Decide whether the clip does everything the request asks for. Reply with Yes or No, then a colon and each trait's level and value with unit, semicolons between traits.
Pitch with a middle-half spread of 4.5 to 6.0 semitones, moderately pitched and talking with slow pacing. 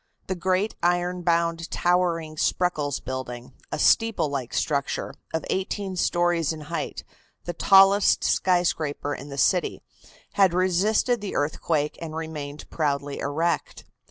No: average, 3.8 semitones; medium, 170 Hz; slow, 130 wpm